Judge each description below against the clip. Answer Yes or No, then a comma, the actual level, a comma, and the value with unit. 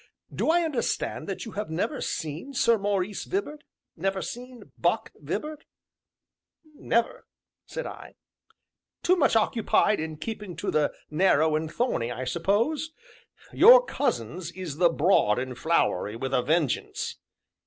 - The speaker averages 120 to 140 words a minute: Yes, slow, 135 wpm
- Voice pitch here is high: Yes, high, 195 Hz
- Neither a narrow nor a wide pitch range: No, wide, 8.1 semitones